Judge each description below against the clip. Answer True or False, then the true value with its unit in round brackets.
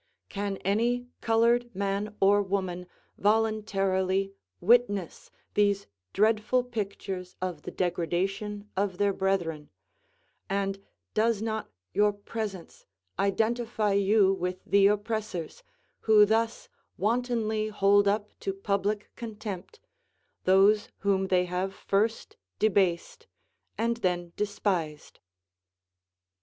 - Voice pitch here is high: True (200 Hz)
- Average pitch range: False (2.2 semitones)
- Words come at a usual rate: False (100 wpm)